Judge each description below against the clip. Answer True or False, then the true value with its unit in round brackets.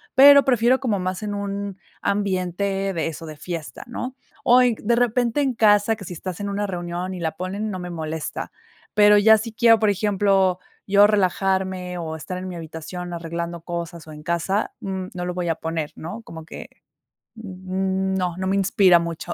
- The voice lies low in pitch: False (190 Hz)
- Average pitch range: True (3.1 semitones)